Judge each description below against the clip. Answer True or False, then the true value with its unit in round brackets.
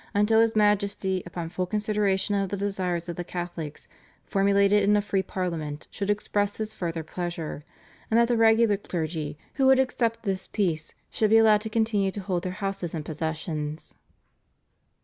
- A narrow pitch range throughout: False (3.4 semitones)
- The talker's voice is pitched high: True (195 Hz)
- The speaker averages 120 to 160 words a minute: False (170 wpm)